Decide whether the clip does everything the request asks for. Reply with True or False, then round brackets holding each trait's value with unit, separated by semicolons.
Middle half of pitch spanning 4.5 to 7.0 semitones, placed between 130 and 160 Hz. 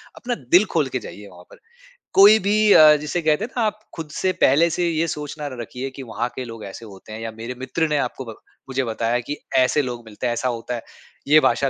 True (5.1 semitones; 135 Hz)